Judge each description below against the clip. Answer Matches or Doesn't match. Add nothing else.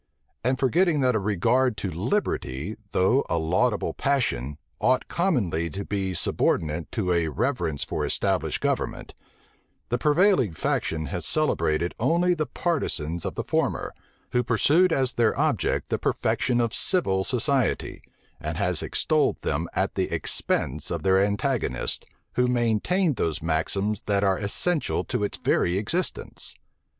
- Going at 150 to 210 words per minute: Doesn't match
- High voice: Doesn't match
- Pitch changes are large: Matches